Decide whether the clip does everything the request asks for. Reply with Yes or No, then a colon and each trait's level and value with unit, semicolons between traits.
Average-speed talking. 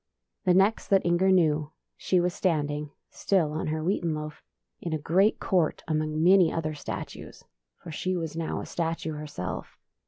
Yes: average, 185 wpm